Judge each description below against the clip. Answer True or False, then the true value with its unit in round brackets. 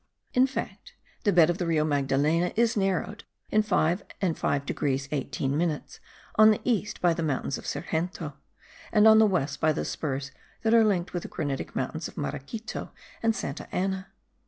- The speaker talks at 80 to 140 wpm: False (180 wpm)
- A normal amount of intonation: False (6.3 semitones)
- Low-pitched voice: False (175 Hz)